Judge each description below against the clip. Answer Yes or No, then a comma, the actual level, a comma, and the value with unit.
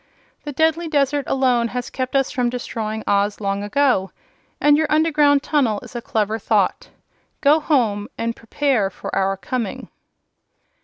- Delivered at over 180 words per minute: No, average, 150 wpm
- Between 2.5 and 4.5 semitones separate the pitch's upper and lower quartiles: No, wide, 5.4 semitones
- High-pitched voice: Yes, very high, 250 Hz